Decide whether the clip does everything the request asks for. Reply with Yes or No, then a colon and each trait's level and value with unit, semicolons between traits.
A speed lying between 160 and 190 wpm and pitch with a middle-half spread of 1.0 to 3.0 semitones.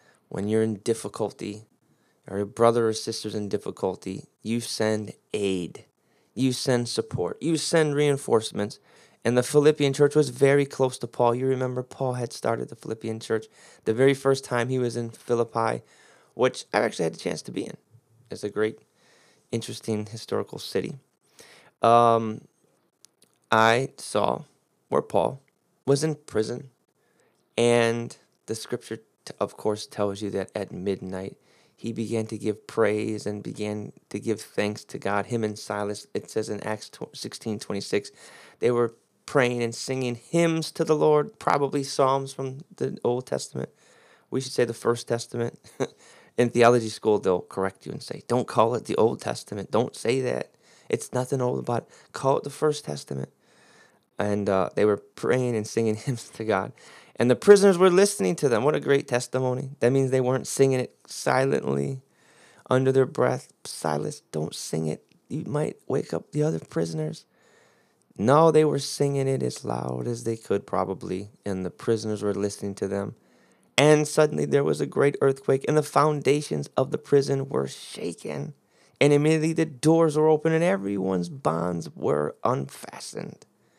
No: average, 165 wpm; average, 4.4 semitones